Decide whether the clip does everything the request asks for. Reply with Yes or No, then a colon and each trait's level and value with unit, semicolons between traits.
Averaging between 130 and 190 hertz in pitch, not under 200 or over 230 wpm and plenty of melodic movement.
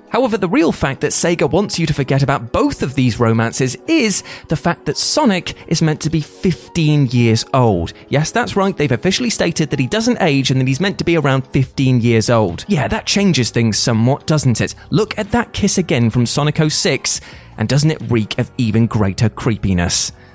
Yes: medium, 140 Hz; fast, 205 wpm; wide, 6.4 semitones